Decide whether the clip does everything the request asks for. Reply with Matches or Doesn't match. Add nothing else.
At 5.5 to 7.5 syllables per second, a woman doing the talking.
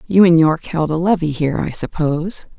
Matches